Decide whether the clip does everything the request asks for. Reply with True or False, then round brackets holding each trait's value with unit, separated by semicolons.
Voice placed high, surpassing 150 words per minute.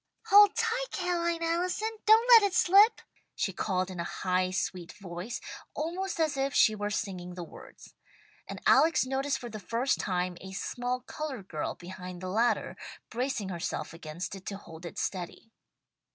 True (225 Hz; 165 wpm)